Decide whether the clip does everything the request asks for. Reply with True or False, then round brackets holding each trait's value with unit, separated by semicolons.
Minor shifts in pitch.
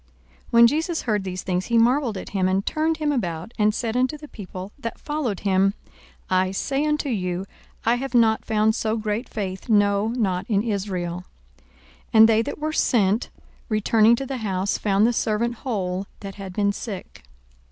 False (3.8 semitones)